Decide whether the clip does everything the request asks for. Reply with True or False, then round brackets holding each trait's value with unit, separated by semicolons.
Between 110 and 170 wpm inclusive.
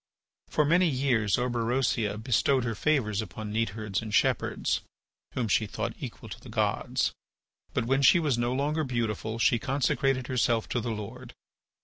True (155 wpm)